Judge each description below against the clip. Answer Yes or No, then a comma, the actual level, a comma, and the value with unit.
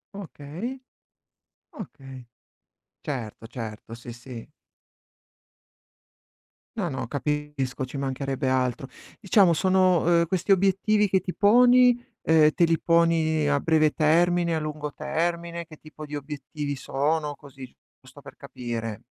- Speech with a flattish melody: No, average, 4.3 semitones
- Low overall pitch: No, medium, 155 Hz